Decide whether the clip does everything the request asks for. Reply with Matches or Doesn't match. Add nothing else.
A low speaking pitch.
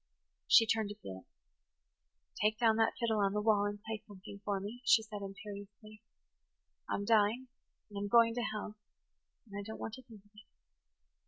Doesn't match